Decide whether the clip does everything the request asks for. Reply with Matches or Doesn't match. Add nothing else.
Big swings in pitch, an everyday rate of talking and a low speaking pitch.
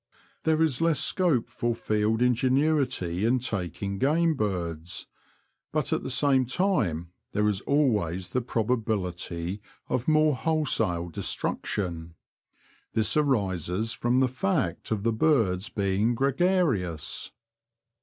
Doesn't match